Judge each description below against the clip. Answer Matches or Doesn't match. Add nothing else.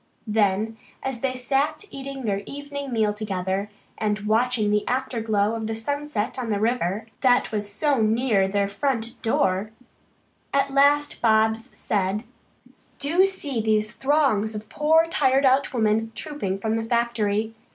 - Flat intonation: Doesn't match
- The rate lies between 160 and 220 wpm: Doesn't match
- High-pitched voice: Matches